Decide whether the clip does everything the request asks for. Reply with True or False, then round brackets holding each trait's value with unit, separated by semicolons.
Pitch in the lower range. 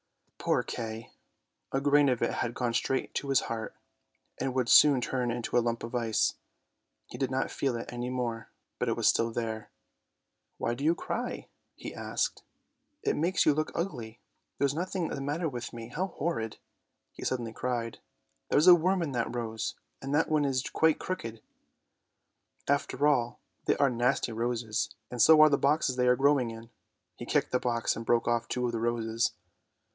True (125 Hz)